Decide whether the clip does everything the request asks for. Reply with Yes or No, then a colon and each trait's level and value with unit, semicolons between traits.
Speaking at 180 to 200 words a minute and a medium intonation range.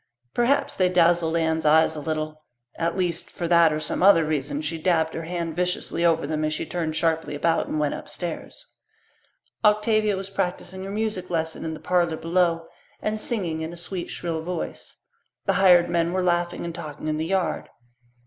No: average, 185 wpm; narrow, 2.3 semitones